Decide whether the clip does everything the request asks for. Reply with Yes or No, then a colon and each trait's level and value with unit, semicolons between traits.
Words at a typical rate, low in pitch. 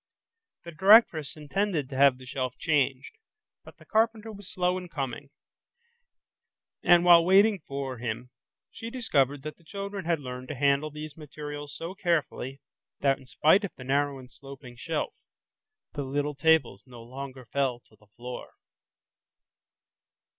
No: average, 150 wpm; medium, 145 Hz